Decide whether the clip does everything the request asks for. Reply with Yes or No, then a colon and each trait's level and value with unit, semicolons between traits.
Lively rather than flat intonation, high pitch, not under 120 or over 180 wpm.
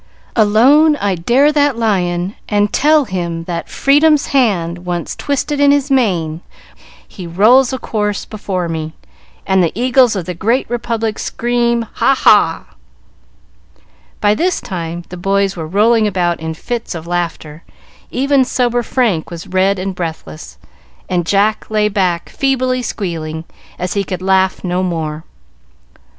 Yes: wide, 5.8 semitones; high, 200 Hz; average, 145 wpm